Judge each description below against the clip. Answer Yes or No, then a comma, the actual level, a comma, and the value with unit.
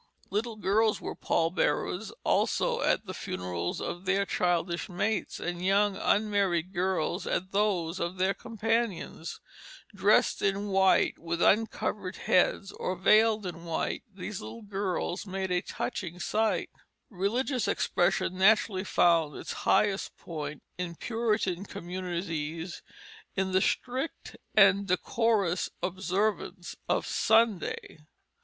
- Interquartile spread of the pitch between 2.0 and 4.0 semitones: Yes, average, 3.1 semitones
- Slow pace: Yes, slow, 120 wpm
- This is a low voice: No, high, 190 Hz